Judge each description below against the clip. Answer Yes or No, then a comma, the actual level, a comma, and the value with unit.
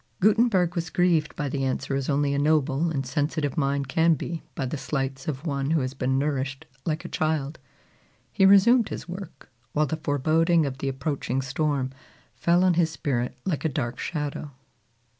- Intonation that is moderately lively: Yes, average, 3.4 semitones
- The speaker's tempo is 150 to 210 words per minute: Yes, average, 180 wpm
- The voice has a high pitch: No, medium, 150 Hz